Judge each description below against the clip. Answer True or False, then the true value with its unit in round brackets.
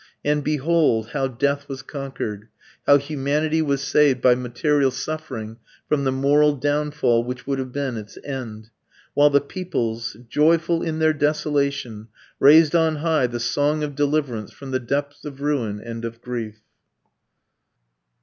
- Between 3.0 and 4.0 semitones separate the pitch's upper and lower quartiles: True (3.5 semitones)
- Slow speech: False (150 wpm)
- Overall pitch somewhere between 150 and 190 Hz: False (140 Hz)